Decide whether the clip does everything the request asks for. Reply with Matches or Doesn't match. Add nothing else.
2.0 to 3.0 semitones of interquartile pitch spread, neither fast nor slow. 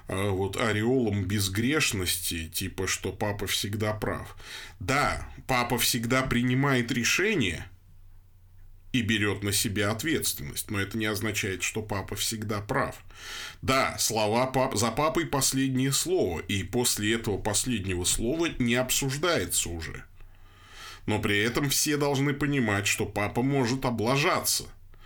Doesn't match